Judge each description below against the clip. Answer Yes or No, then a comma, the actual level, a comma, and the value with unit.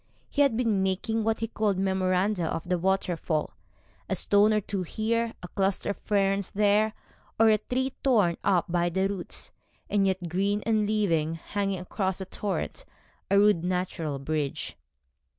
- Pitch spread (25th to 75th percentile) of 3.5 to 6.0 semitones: No, average, 2.9 semitones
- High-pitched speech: Yes, high, 195 Hz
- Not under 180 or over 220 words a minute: No, average, 165 wpm